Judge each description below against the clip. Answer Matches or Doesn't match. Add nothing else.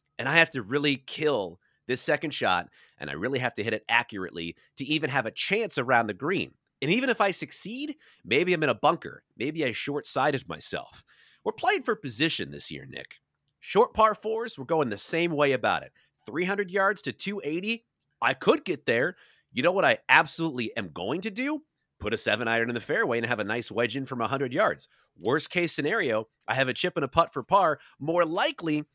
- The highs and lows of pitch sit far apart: Matches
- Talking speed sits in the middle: Doesn't match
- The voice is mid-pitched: Matches